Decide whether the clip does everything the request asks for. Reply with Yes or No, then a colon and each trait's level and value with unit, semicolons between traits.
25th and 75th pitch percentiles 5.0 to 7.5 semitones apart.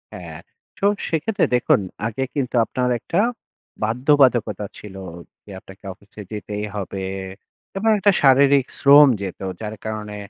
Yes: average, 5.3 semitones